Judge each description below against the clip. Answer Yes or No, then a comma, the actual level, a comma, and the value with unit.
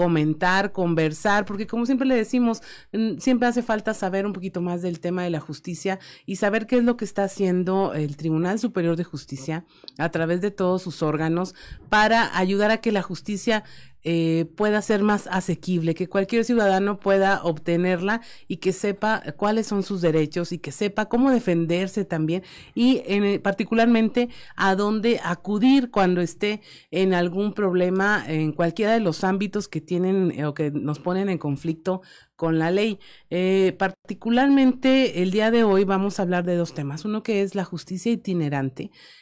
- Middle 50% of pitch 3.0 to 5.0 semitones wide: Yes, average, 3.7 semitones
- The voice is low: No, high, 190 Hz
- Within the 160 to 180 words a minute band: Yes, average, 175 wpm